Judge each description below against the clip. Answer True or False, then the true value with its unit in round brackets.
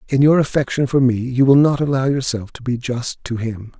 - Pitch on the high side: False (130 Hz)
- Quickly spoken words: True (235 wpm)